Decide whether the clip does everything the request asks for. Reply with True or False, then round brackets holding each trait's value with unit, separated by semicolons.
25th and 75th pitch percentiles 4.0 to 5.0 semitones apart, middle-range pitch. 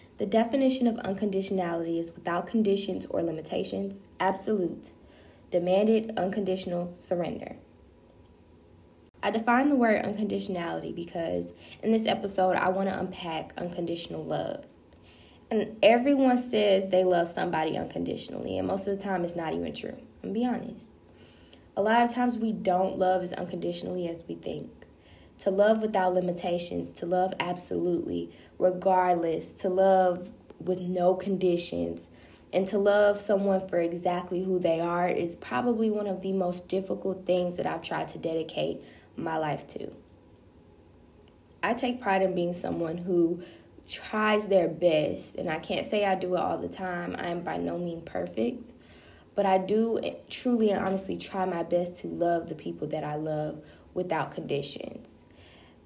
False (3.0 semitones; 180 Hz)